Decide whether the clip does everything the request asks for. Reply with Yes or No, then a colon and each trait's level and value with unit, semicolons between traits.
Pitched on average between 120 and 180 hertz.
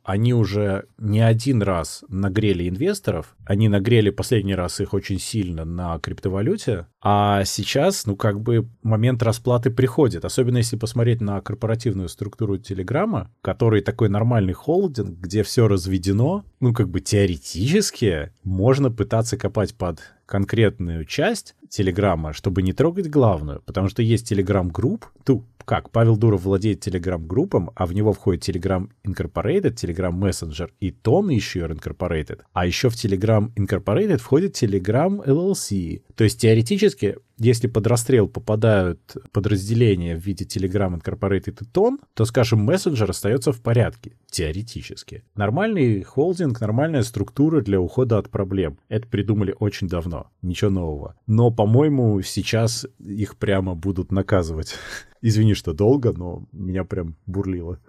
No: low, 105 Hz